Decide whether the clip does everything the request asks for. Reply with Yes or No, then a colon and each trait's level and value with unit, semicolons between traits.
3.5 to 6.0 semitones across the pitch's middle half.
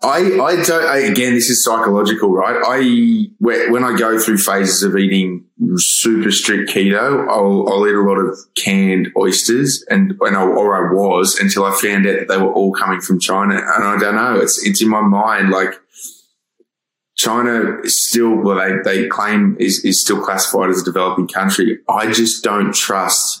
No: average, 2.8 semitones